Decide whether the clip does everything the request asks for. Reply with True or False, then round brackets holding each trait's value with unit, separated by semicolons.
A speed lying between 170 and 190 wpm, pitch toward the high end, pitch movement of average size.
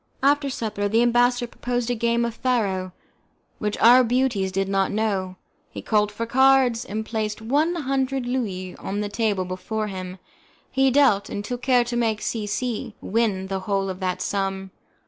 True (175 wpm; 220 Hz; 3.9 semitones)